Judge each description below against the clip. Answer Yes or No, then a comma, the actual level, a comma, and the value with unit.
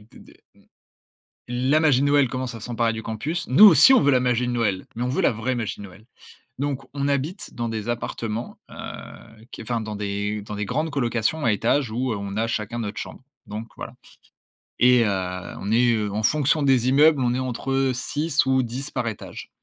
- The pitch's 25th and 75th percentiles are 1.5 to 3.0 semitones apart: No, average, 3.7 semitones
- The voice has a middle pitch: No, low, 120 Hz